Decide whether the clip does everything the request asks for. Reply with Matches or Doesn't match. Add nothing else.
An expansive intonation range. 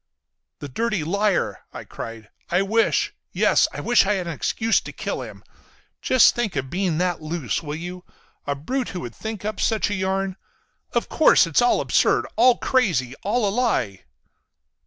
Matches